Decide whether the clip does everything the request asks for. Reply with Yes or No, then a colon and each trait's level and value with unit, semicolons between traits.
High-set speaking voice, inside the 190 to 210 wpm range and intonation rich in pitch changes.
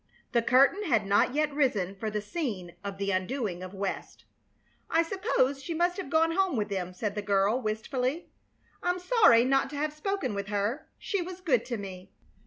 Yes: very high, 250 Hz; average, 195 wpm; wide, 8.3 semitones